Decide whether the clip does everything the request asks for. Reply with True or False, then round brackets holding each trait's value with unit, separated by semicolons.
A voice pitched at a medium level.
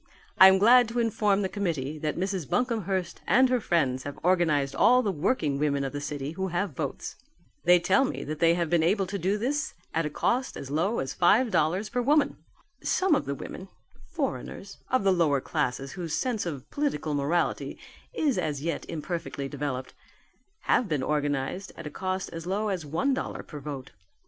True (175 Hz)